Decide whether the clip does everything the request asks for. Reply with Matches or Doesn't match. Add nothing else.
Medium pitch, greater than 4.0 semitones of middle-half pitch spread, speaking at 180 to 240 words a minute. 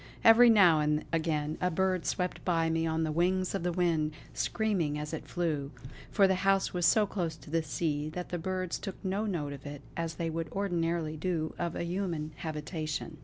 Doesn't match